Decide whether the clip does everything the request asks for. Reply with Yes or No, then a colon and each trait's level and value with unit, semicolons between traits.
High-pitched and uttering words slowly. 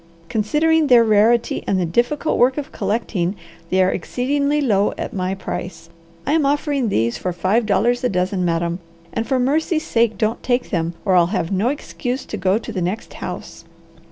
No: high, 220 Hz; average, 185 wpm